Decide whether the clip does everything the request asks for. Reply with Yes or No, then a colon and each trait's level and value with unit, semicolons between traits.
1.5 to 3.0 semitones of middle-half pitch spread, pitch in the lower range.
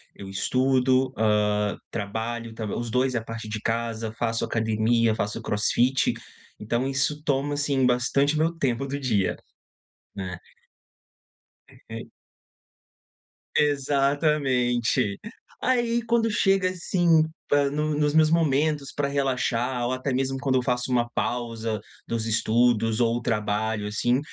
No: average, 4.0 semitones; low, 125 Hz